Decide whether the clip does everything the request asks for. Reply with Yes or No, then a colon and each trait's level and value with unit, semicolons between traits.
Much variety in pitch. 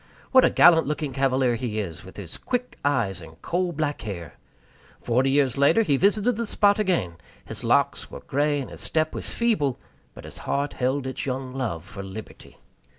Yes: wide, 6.1 semitones